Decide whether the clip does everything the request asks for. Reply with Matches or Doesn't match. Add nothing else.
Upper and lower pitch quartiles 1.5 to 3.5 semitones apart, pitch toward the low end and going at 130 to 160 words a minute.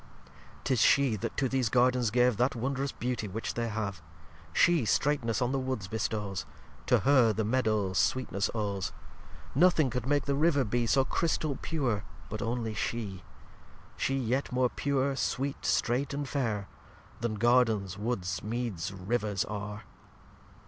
Doesn't match